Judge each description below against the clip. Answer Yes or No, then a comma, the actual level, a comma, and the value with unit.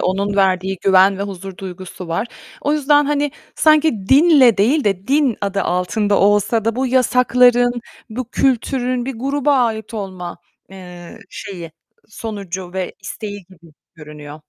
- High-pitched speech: Yes, high, 205 Hz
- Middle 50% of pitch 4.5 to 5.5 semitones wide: Yes, average, 5.2 semitones